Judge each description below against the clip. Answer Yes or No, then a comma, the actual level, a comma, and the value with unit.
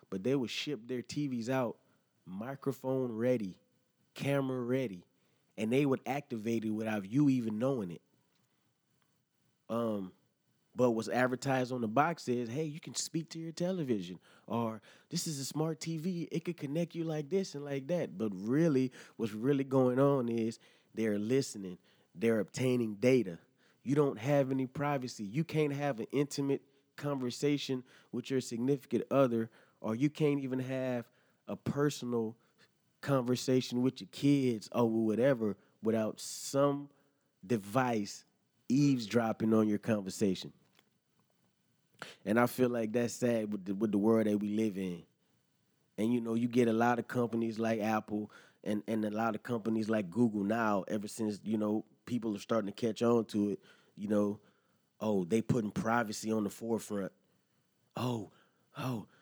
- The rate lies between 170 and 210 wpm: No, average, 160 wpm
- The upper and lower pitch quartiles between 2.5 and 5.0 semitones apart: Yes, average, 3.9 semitones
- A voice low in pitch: Yes, low, 120 Hz